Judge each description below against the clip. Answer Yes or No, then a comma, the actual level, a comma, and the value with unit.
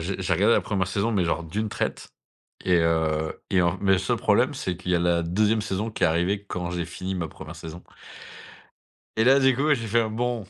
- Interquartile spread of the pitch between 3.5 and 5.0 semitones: Yes, average, 4.0 semitones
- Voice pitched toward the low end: Yes, very low, 95 Hz